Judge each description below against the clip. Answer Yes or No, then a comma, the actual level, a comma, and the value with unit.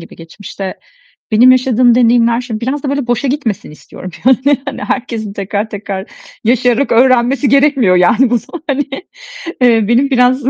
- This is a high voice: Yes, high, 245 Hz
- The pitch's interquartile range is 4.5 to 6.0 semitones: No, average, 3.5 semitones